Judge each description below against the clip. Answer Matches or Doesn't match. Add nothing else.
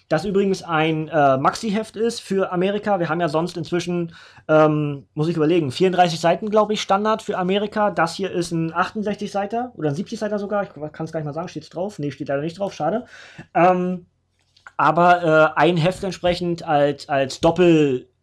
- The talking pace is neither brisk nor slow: Doesn't match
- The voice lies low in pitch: Doesn't match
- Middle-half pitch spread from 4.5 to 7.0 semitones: Doesn't match